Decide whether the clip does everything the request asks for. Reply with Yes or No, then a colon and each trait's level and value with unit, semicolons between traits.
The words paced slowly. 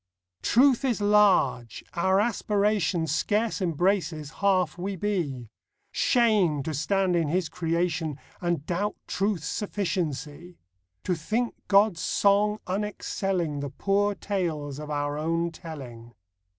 Yes: slow, 115 wpm